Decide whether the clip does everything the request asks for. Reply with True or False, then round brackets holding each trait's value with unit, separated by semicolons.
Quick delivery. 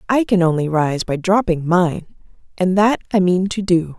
False (195 wpm)